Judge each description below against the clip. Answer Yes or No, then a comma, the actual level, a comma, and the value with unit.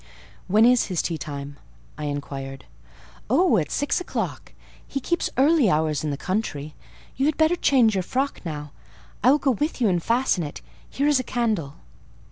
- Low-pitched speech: No, high, 215 Hz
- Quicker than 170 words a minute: Yes, average, 180 wpm